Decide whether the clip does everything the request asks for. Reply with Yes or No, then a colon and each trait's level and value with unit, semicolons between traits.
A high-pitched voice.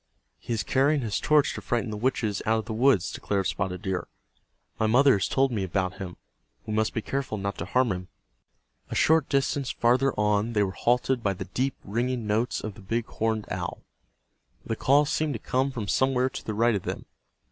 No: low, 115 Hz